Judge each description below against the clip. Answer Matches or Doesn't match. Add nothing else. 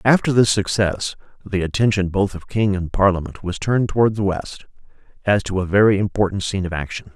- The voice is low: Matches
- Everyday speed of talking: Matches